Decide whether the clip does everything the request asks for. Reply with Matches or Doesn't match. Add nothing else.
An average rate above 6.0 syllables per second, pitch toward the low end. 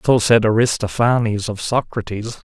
Doesn't match